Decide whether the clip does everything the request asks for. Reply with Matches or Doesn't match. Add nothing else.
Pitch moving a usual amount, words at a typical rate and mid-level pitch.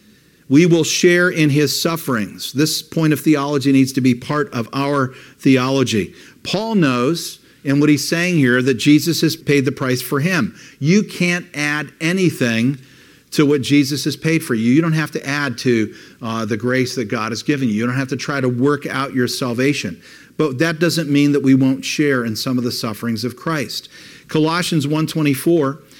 Matches